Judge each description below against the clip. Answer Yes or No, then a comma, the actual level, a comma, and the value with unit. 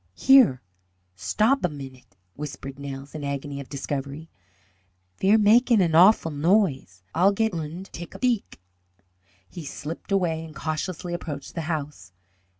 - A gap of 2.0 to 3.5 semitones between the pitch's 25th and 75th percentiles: No, average, 5.3 semitones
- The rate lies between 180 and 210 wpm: No, average, 140 wpm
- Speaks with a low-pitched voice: No, medium, 160 Hz